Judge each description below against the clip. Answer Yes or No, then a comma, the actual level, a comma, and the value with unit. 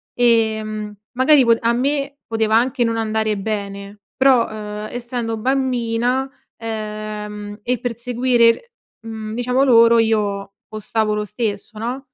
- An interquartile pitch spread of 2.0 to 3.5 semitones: Yes, narrow, 2.5 semitones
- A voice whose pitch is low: No, high, 225 Hz